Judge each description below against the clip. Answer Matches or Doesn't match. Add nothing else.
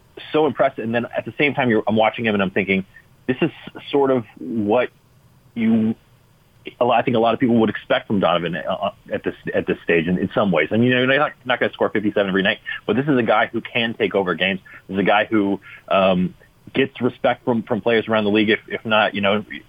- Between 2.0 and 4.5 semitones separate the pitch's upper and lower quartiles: Matches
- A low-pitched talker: Matches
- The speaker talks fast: Matches